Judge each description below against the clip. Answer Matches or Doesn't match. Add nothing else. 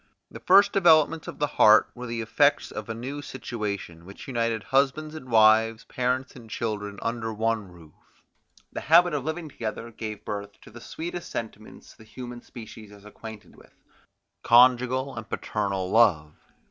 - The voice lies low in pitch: Matches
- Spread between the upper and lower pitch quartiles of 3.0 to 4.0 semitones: Matches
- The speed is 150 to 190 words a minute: Matches